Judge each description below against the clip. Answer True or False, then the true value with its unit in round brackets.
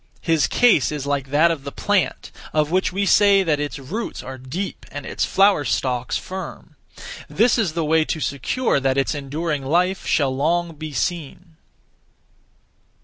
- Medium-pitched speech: True (155 Hz)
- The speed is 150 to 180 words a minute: True (165 wpm)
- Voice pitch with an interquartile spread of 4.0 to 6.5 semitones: True (4.6 semitones)